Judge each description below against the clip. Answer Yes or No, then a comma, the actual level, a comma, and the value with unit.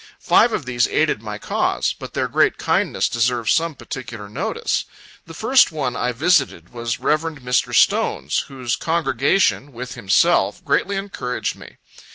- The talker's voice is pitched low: Yes, low, 125 Hz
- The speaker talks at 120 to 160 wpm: Yes, average, 150 wpm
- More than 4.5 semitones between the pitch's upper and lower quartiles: Yes, average, 5.1 semitones